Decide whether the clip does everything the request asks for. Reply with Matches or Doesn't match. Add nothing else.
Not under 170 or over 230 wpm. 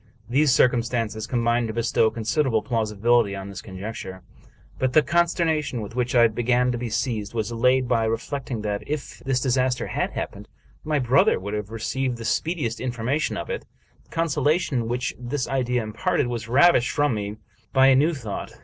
Matches